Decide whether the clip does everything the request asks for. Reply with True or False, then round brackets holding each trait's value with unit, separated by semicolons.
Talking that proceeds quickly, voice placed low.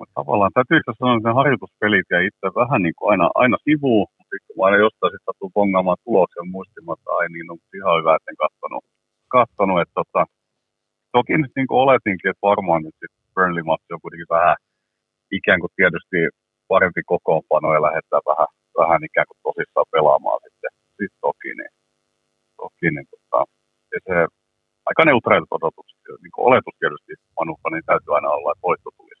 True (175 wpm; 125 Hz)